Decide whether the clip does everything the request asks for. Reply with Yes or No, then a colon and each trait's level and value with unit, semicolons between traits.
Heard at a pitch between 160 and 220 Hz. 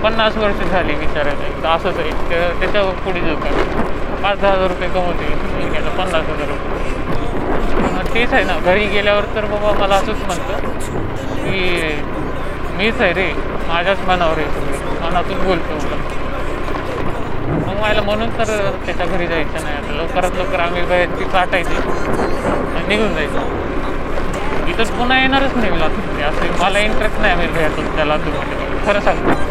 Yes: medium, 185 Hz